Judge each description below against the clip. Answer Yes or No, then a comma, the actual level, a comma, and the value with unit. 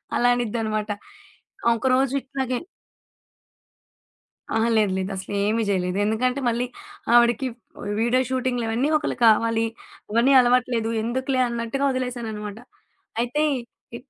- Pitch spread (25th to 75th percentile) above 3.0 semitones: No, narrow, 2.6 semitones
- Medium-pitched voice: No, high, 235 Hz